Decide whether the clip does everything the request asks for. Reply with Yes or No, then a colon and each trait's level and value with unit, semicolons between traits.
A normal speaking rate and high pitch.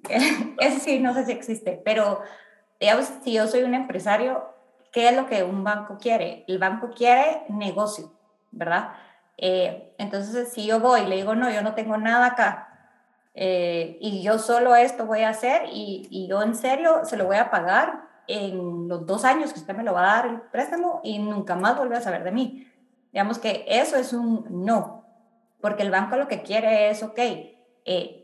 No: fast, 200 wpm; high, 220 Hz